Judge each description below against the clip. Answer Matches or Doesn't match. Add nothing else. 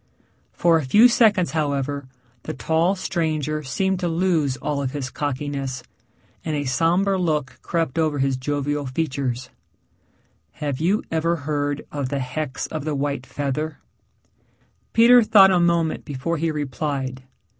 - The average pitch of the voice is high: Doesn't match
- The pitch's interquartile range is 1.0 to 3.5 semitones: Matches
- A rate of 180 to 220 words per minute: Doesn't match